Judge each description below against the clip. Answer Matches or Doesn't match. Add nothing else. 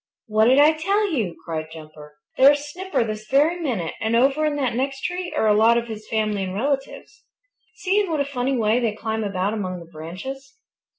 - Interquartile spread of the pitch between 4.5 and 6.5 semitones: Matches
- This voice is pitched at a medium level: Doesn't match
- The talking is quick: Matches